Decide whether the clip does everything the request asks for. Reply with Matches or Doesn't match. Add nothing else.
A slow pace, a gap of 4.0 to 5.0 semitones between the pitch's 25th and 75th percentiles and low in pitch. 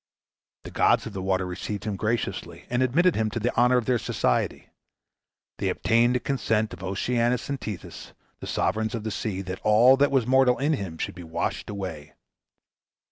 Doesn't match